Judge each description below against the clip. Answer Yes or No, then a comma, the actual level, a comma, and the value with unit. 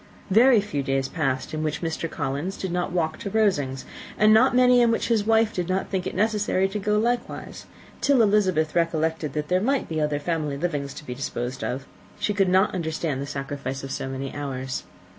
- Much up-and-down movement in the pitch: Yes, wide, 6.7 semitones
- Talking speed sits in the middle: No, fast, 210 wpm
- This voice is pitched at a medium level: Yes, medium, 165 Hz